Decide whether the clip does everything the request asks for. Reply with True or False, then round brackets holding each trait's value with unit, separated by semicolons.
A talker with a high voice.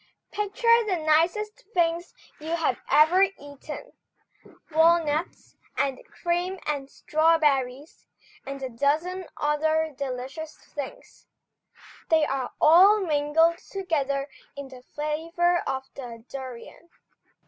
True (310 Hz)